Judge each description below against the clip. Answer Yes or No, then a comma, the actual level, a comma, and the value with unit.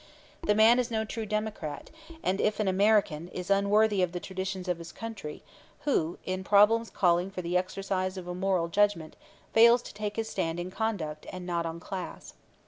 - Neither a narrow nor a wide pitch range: Yes, average, 3.2 semitones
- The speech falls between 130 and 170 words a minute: No, average, 190 wpm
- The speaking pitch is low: No, high, 190 Hz